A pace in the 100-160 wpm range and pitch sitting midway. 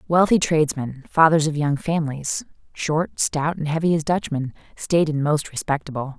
Yes: average, 155 wpm; medium, 155 Hz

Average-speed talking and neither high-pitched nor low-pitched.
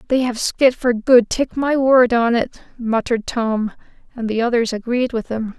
No: average, 195 wpm; high, 235 Hz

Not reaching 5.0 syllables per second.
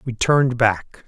Yes: 4.3 syllables/s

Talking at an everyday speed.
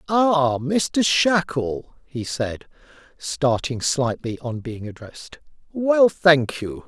No: slow, 115 wpm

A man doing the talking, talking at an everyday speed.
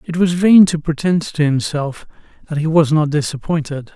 Yes: male; average, 180 wpm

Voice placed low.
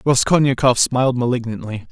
Yes: low, 125 Hz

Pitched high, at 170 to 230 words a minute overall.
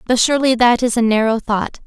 Yes: high, 235 Hz; fast, 225 wpm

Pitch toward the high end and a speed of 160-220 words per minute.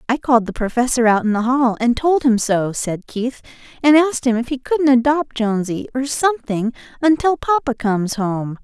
Yes: very high, 250 Hz; average, 195 wpm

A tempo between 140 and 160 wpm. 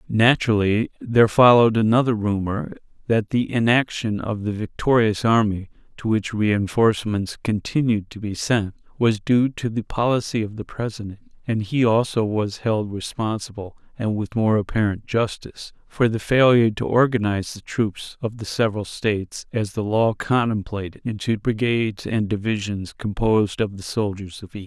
Yes: average, 155 wpm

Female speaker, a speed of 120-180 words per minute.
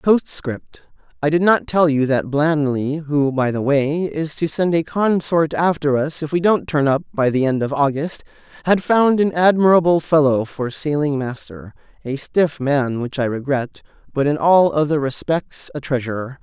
No: male; average, 175 wpm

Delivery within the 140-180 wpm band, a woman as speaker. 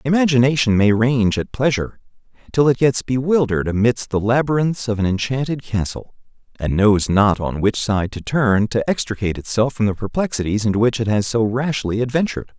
No: average, 175 wpm; male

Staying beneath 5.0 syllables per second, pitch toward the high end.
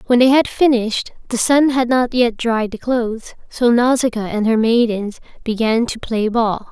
Yes: 4.7 syllables/s; high, 235 Hz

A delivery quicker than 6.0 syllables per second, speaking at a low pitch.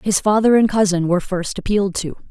No: 6.2 syllables/s; high, 195 Hz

